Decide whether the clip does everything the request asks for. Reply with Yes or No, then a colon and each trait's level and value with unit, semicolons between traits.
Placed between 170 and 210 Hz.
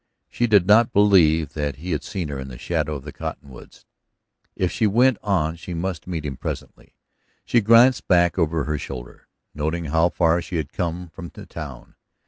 No: very low, 85 Hz